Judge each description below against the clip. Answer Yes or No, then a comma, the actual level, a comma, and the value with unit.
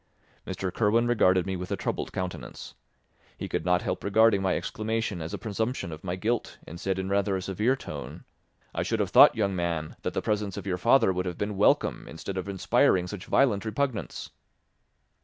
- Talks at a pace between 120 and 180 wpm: No, average, 195 wpm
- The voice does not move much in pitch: No, average, 3.0 semitones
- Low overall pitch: Yes, very low, 95 Hz